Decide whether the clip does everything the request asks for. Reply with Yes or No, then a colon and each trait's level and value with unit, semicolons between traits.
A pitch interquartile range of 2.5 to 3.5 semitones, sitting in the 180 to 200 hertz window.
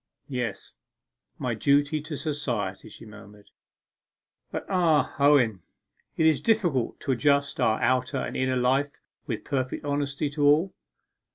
No: average, 3.0 semitones; medium, 140 Hz